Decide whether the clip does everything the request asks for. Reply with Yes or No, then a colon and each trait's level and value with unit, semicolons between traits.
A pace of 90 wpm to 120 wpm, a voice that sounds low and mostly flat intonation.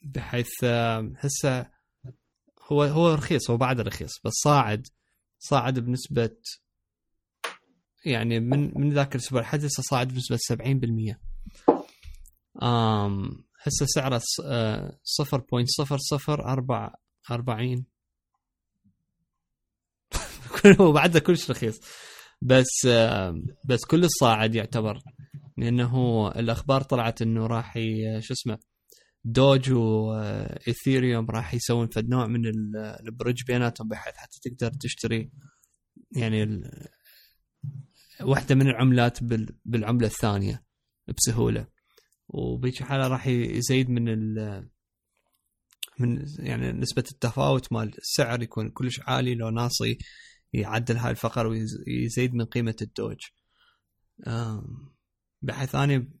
No: average, 100 wpm; low, 120 Hz; average, 3.1 semitones